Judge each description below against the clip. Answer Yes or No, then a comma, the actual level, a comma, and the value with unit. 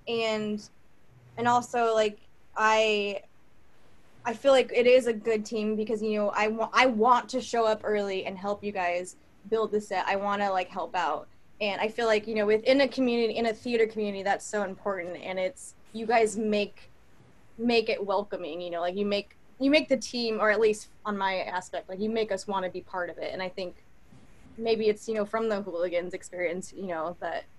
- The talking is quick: Yes, fast, 220 wpm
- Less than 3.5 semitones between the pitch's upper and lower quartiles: Yes, average, 2.8 semitones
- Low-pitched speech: No, high, 215 Hz